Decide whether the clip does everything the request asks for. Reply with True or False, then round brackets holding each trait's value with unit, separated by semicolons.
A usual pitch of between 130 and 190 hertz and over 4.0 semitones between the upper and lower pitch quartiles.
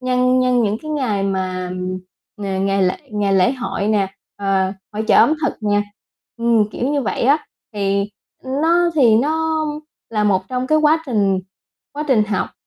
False (215 Hz; 5.0 semitones)